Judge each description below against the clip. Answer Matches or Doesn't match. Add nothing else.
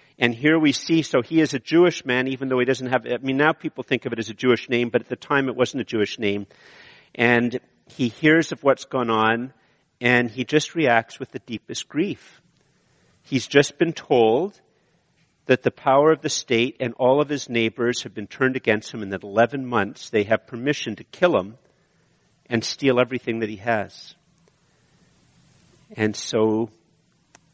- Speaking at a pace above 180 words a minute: Matches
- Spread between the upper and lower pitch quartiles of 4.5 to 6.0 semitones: Doesn't match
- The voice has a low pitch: Matches